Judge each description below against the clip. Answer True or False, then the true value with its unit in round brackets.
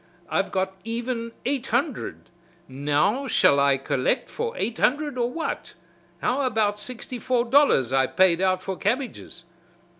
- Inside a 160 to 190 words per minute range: False (145 wpm)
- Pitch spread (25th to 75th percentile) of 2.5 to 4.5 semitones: False (5.6 semitones)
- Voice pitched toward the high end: True (230 Hz)